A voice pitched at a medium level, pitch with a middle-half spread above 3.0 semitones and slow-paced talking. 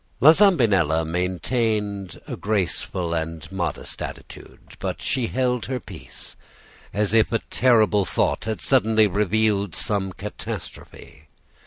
No: low, 105 Hz; average, 3.8 semitones; slow, 120 wpm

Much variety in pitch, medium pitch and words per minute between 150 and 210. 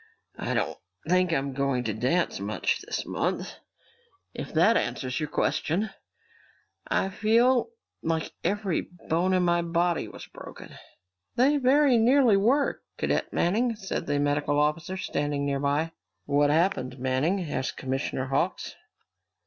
No: wide, 6.0 semitones; medium, 165 Hz; slow, 135 wpm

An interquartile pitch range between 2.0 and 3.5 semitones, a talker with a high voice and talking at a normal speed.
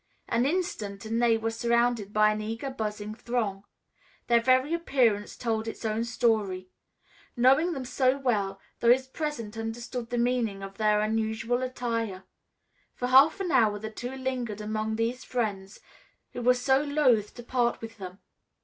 Yes: average, 2.9 semitones; high, 230 Hz; average, 160 wpm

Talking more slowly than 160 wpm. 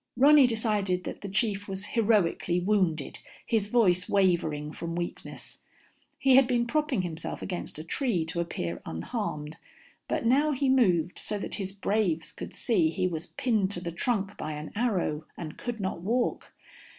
No: average, 165 wpm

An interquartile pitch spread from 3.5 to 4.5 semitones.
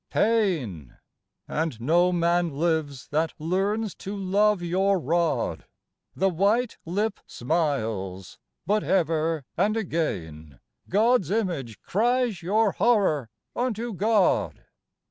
No: wide, 5.4 semitones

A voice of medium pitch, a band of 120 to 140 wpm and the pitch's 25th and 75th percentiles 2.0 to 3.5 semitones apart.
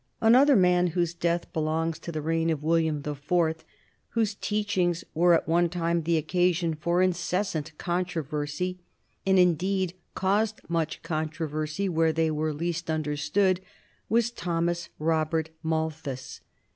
Yes: medium, 170 Hz; slow, 135 wpm; narrow, 2.4 semitones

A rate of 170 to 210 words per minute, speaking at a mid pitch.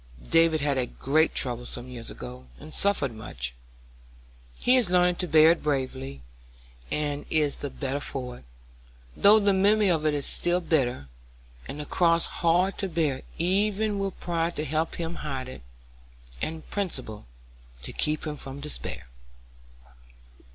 No: average, 155 wpm; medium, 155 Hz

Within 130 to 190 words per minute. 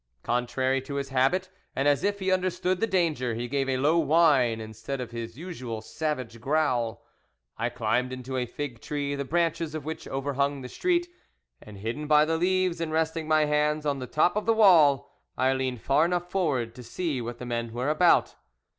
No: average, 200 wpm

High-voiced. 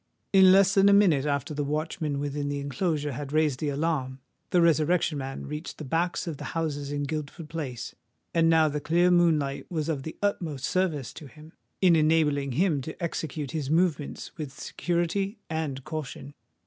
No: medium, 155 Hz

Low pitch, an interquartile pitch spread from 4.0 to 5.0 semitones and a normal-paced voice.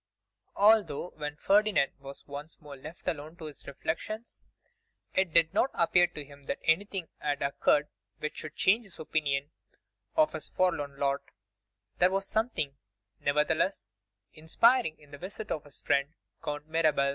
No: medium, 155 Hz; average, 4.6 semitones; average, 150 wpm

